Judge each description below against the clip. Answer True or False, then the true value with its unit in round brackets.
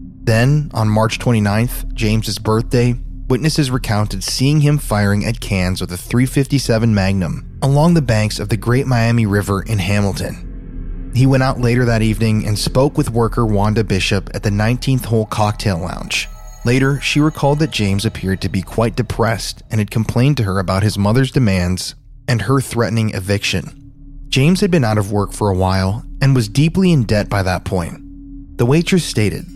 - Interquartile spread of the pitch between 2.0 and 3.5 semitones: False (4.6 semitones)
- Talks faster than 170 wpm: True (180 wpm)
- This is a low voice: True (115 Hz)